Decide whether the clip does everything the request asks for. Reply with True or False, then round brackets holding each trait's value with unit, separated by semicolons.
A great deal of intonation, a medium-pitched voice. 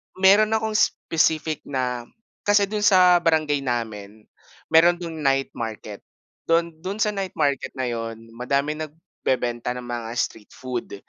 True (6.5 semitones; 145 Hz)